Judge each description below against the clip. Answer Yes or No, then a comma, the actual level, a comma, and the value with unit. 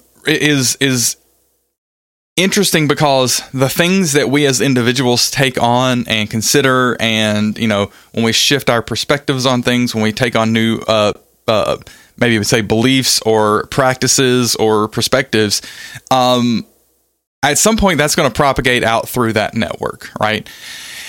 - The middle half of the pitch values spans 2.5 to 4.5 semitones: Yes, average, 4.0 semitones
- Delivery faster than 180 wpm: No, average, 150 wpm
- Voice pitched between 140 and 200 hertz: No, low, 125 Hz